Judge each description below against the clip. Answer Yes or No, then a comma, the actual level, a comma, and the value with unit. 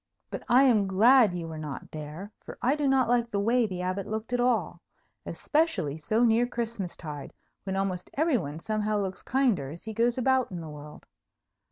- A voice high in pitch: Yes, high, 215 Hz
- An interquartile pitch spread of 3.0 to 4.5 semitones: No, wide, 5.6 semitones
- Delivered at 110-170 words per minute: No, average, 200 wpm